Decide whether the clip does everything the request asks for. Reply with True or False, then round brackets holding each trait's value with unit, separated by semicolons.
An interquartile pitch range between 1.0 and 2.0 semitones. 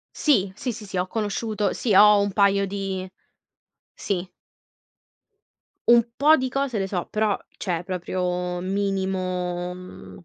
False (2.5 semitones)